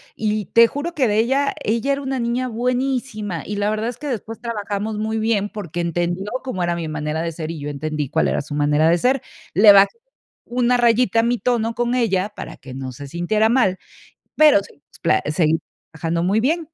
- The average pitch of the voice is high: Yes, high, 210 Hz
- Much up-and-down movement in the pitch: Yes, wide, 6.1 semitones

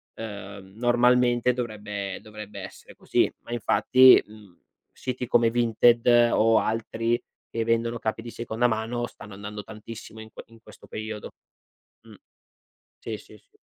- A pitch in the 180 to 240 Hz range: No, low, 115 Hz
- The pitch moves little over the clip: Yes, narrow, 1.9 semitones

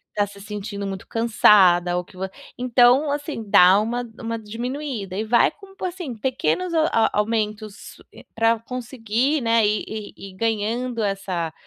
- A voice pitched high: Yes, high, 225 Hz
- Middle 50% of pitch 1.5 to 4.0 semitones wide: Yes, average, 3.5 semitones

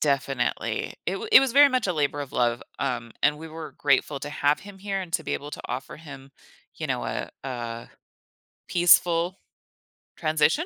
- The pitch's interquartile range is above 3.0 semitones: Yes, average, 4.6 semitones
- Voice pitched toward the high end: No, medium, 150 Hz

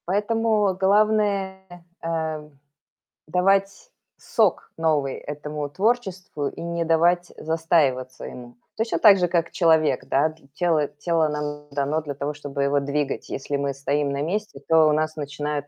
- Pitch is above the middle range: No, medium, 160 Hz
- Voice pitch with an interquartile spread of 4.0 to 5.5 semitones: Yes, average, 4.3 semitones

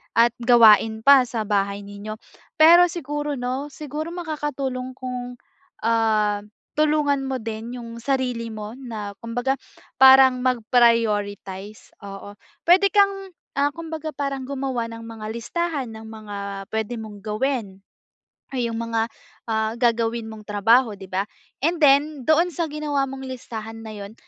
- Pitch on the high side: Yes, high, 240 Hz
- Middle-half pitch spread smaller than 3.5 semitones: No, average, 4.3 semitones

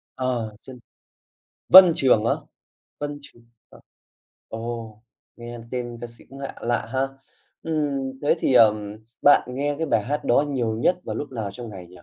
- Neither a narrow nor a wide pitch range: Yes, average, 3.8 semitones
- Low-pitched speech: Yes, low, 120 Hz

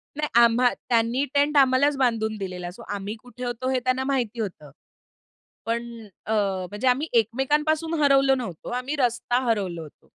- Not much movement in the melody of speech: No, average, 3.5 semitones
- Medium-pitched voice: No, high, 245 Hz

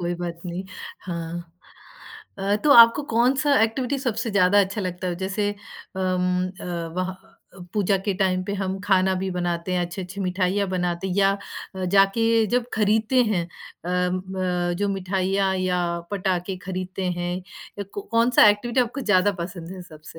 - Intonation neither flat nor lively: No, narrow, 2.3 semitones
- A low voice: No, high, 190 Hz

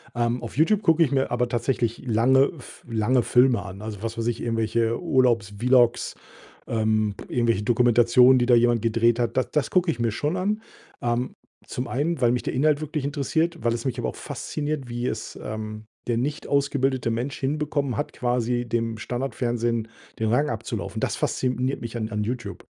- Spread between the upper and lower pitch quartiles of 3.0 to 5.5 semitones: No, narrow, 2.6 semitones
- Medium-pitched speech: No, low, 120 Hz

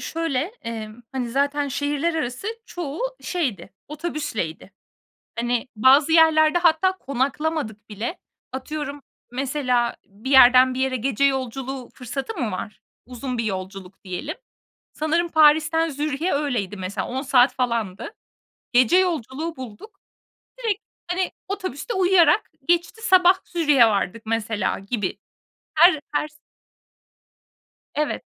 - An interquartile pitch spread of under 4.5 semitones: No, average, 5.3 semitones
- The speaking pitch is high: Yes, very high, 275 Hz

